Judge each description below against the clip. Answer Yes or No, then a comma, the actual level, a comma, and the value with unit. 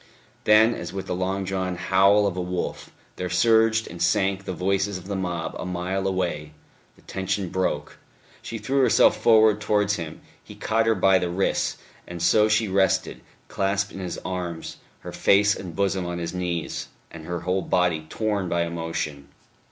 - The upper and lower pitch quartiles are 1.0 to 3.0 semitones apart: Yes, narrow, 2.5 semitones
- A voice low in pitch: Yes, very low, 95 Hz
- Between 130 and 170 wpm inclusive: No, average, 180 wpm